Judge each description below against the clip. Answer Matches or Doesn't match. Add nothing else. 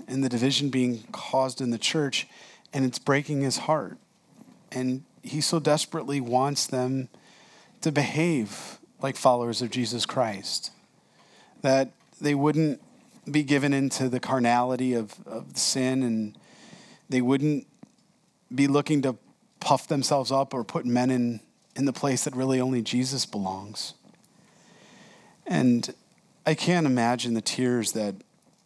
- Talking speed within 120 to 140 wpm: Matches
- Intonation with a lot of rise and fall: Doesn't match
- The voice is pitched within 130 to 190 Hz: Matches